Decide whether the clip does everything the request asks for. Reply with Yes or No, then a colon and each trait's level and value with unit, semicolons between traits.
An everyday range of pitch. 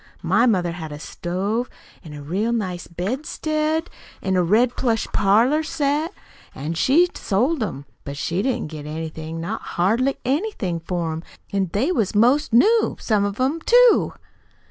No: wide, 7.9 semitones